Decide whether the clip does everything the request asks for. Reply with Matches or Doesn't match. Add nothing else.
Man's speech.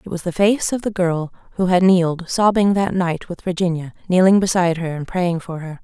Doesn't match